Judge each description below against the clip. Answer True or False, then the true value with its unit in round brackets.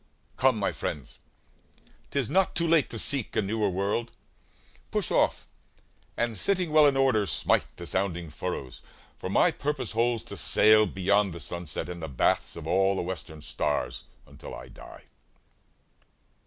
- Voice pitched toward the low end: True (100 Hz)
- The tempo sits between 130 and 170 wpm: True (160 wpm)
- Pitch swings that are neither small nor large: False (5.9 semitones)